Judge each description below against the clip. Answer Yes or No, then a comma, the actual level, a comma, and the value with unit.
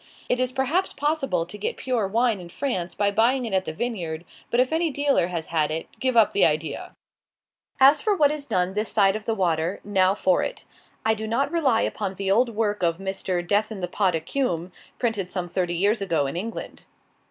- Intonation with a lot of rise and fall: Yes, wide, 5.8 semitones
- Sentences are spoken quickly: Yes, fast, 215 wpm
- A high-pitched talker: Yes, high, 205 Hz